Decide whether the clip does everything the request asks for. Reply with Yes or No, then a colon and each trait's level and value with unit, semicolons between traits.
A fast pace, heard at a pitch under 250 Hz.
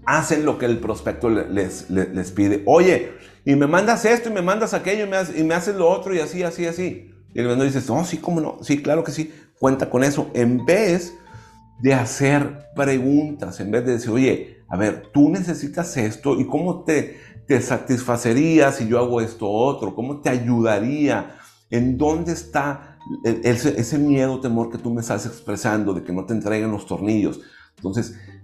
Yes: fast, 205 wpm; low, 135 Hz